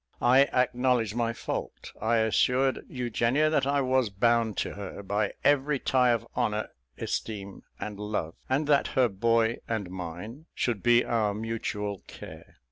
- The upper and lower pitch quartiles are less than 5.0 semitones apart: Yes, average, 3.4 semitones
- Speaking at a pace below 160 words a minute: Yes, average, 150 wpm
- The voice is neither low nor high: No, low, 115 Hz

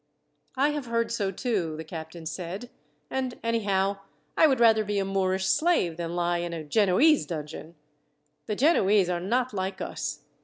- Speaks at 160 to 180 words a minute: Yes, average, 165 wpm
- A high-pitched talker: Yes, high, 195 Hz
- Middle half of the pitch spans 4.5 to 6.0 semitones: Yes, average, 5.1 semitones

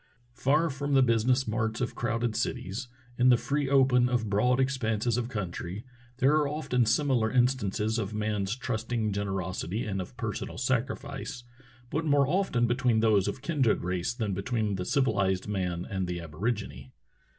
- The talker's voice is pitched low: Yes, low, 115 Hz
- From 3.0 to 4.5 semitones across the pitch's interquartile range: Yes, average, 4.1 semitones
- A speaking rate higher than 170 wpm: No, average, 160 wpm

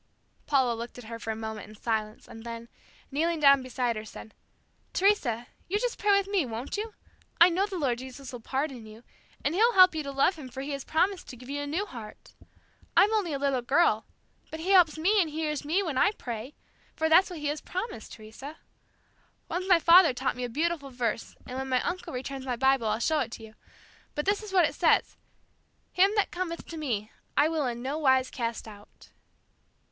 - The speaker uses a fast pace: Yes, fast, 220 wpm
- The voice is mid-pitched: No, very high, 280 Hz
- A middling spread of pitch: No, wide, 6.2 semitones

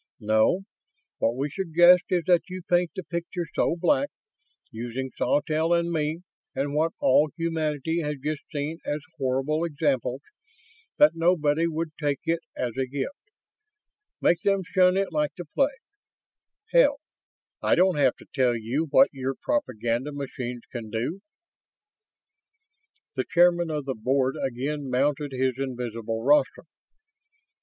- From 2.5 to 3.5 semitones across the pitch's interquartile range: No, average, 4.5 semitones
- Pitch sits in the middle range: Yes, medium, 150 Hz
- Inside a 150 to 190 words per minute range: No, average, 140 wpm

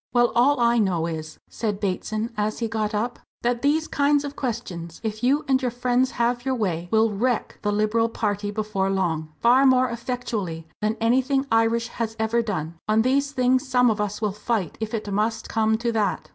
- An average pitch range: Yes, average, 3.0 semitones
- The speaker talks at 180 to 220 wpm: Yes, average, 200 wpm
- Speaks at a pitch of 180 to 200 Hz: No, high, 225 Hz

